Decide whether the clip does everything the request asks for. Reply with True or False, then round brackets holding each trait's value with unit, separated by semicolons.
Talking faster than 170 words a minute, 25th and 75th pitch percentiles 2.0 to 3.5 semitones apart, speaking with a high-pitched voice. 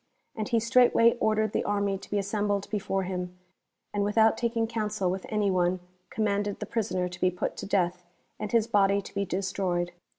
True (190 wpm; 2.6 semitones; 200 Hz)